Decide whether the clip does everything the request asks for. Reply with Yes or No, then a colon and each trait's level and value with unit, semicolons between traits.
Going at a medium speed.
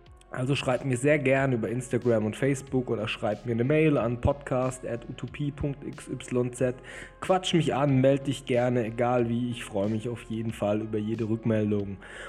Yes: average, 165 wpm